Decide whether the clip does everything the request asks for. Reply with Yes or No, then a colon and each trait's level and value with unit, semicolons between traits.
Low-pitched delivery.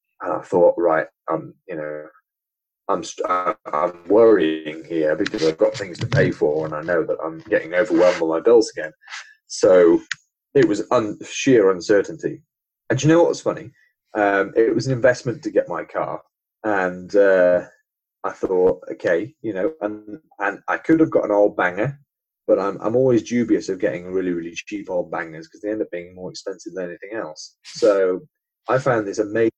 Yes: low, 115 Hz